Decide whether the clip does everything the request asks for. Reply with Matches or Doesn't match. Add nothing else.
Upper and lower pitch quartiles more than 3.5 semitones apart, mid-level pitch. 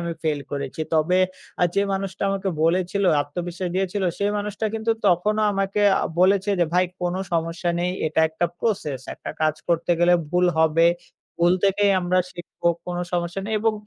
Doesn't match